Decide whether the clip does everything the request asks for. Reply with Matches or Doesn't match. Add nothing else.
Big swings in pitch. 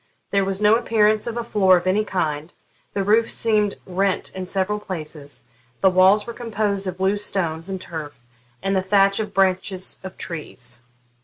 Doesn't match